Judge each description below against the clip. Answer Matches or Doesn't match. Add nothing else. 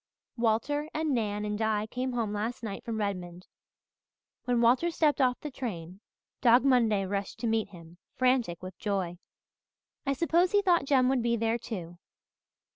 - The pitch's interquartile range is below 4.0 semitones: Doesn't match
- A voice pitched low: Doesn't match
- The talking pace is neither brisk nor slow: Matches